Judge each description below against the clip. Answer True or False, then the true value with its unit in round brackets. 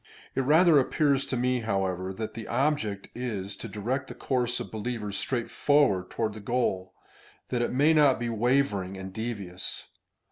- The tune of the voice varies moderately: True (4.7 semitones)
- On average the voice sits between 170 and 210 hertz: False (120 Hz)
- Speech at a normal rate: True (170 wpm)